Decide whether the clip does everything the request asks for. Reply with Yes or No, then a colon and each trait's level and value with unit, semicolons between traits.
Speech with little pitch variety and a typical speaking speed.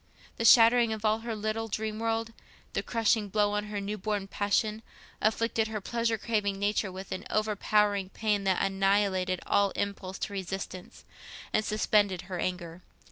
Yes: narrow, 2.0 semitones; average, 160 wpm